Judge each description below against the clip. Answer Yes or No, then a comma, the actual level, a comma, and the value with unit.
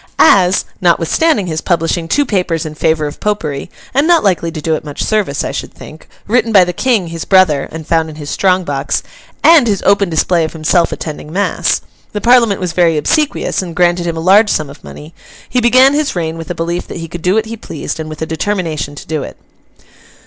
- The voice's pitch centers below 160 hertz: No, medium, 175 Hz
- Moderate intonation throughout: Yes, average, 4.4 semitones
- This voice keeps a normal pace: No, fast, 215 wpm